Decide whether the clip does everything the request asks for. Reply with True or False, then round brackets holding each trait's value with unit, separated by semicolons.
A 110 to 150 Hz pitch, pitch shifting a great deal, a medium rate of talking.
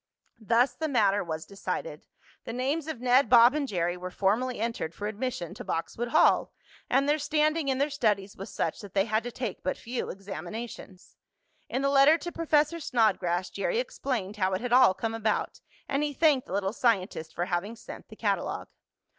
False (230 Hz; 6.1 semitones; 190 wpm)